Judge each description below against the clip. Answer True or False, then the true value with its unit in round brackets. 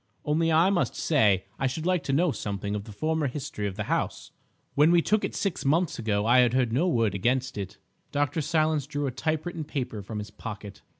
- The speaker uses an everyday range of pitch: False (6.8 semitones)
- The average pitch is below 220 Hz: True (135 Hz)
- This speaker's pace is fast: True (215 wpm)